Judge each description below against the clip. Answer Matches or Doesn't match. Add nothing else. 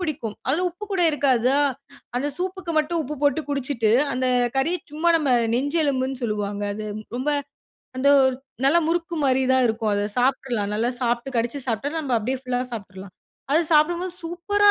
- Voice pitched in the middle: Doesn't match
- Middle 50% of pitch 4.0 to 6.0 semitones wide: Matches